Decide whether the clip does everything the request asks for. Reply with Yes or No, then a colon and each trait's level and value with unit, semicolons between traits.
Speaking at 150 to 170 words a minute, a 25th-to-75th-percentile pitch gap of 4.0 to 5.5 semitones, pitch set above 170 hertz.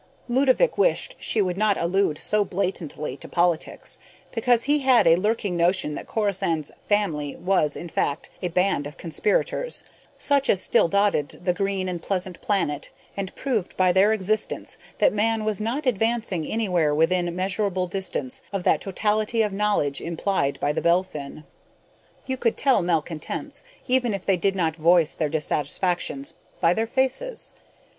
Yes: average, 155 wpm; average, 4.3 semitones; high, 190 Hz